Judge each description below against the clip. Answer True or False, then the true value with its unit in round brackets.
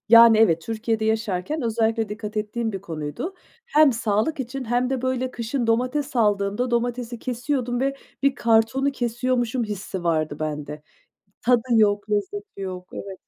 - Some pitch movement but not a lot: True (3.5 semitones)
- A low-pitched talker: False (230 Hz)